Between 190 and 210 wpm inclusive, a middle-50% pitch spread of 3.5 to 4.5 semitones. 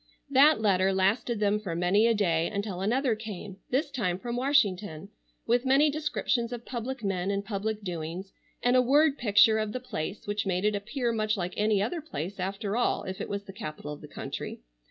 Yes: average, 200 wpm; average, 4.1 semitones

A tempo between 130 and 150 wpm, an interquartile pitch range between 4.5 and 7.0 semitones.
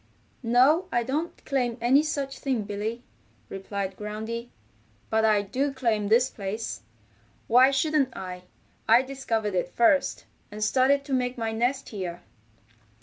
No: average, 140 wpm; average, 4.1 semitones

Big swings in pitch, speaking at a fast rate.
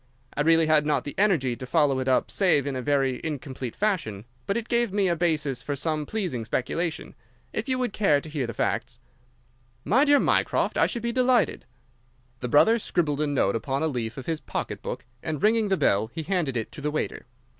Yes: wide, 6.6 semitones; fast, 215 wpm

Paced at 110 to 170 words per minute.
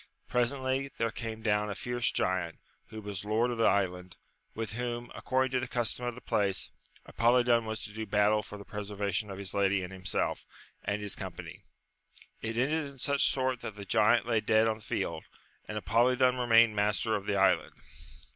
No: average, 195 wpm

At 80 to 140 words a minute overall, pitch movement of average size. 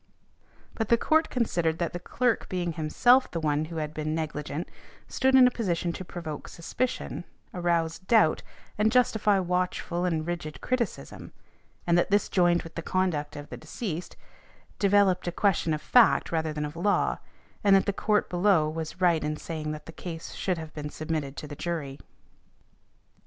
No: average, 175 wpm; average, 4.1 semitones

